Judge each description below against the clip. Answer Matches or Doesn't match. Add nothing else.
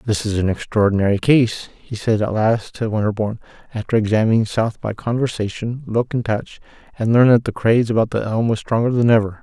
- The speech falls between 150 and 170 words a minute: Doesn't match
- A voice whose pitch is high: Doesn't match